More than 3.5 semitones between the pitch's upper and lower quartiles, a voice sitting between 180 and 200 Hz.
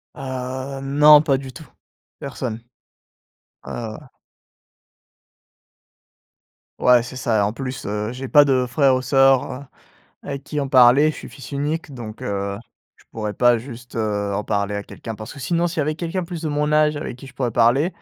No: average, 4.0 semitones; low, 130 Hz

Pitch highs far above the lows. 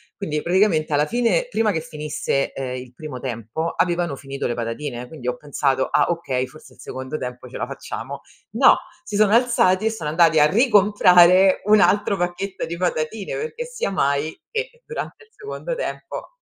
Yes: wide, 7.1 semitones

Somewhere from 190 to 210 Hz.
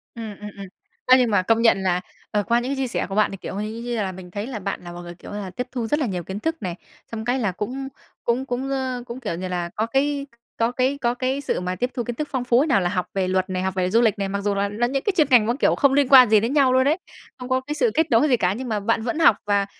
No: high, 230 Hz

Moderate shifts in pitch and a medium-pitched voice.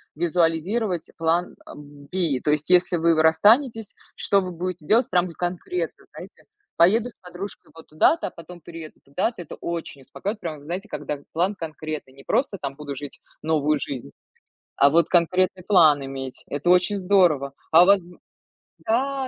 Yes: average, 3.7 semitones; medium, 170 Hz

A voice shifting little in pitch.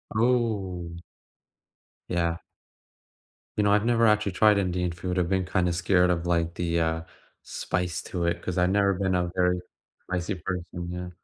Yes: narrow, 2.1 semitones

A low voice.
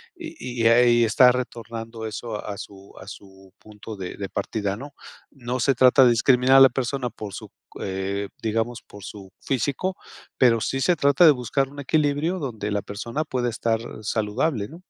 Yes: low, 120 Hz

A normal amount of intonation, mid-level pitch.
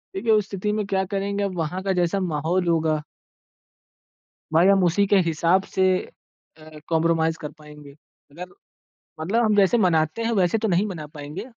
Yes: average, 3.9 semitones; medium, 180 Hz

